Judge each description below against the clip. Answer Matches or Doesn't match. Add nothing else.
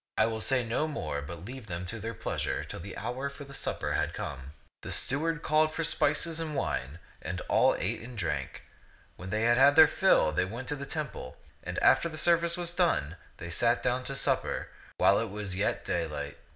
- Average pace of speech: Doesn't match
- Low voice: Matches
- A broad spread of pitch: Matches